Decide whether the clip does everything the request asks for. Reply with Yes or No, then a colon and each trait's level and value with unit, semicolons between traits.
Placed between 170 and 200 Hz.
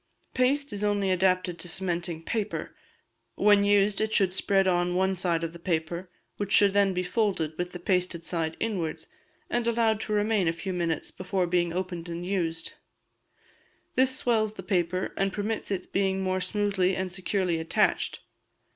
Yes: medium, 185 Hz